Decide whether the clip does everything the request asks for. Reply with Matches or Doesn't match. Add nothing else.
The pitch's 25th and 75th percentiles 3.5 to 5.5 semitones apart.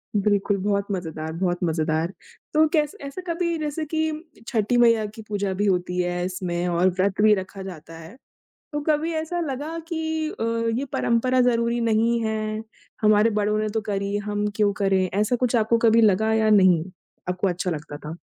Matches